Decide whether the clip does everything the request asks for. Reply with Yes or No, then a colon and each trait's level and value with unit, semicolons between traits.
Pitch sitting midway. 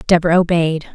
Yes: medium, 170 Hz